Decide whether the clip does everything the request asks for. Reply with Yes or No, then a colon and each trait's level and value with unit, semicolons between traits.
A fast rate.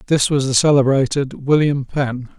No: average, 150 wpm